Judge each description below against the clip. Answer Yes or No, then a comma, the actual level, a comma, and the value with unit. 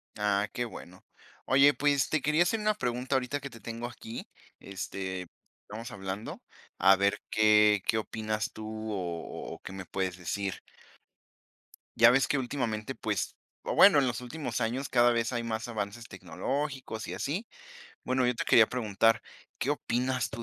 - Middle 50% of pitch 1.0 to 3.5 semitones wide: No, average, 3.9 semitones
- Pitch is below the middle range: Yes, low, 115 Hz